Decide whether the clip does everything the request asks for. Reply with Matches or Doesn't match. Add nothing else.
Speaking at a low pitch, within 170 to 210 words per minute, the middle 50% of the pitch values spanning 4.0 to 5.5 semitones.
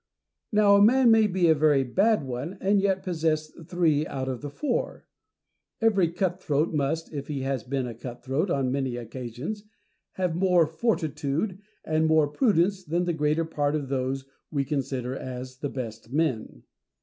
Doesn't match